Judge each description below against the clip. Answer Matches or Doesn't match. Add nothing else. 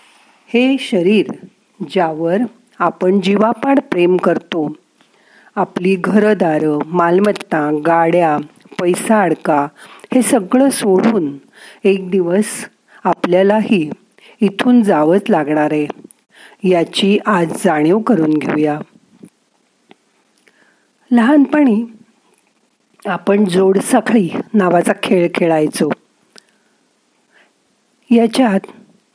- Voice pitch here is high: Matches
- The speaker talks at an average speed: Doesn't match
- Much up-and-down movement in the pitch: Doesn't match